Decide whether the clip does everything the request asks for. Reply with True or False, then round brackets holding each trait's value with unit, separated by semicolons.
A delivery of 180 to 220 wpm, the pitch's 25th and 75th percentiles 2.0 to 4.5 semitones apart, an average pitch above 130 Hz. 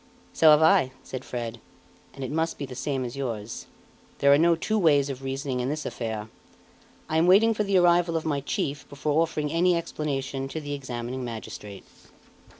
True (190 wpm; 3.9 semitones; 140 Hz)